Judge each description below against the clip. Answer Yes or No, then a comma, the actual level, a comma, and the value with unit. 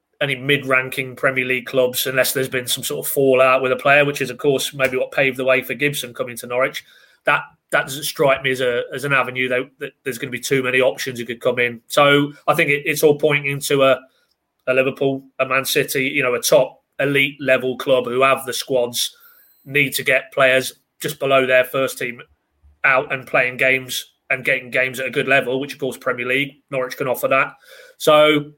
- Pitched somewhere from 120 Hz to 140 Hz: Yes, low, 135 Hz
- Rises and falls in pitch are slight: Yes, narrow, 1.8 semitones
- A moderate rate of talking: No, fast, 225 wpm